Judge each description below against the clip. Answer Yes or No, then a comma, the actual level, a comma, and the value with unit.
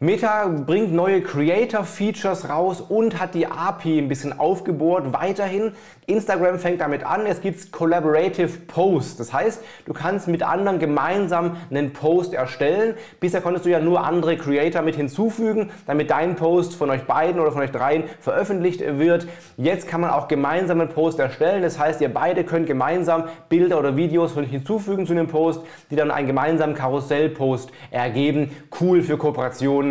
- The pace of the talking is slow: No, average, 165 wpm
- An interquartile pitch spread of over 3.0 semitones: Yes, average, 3.6 semitones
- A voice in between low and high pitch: Yes, medium, 165 Hz